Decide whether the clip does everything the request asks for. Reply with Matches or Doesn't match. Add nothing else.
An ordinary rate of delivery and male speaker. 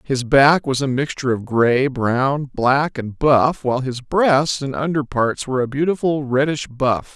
Matches